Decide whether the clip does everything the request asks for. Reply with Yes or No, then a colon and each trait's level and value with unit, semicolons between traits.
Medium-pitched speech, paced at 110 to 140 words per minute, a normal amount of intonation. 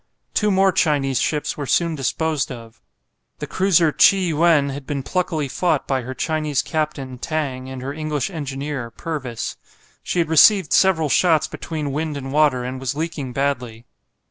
No: medium, 150 Hz; average, 165 wpm; average, 3.3 semitones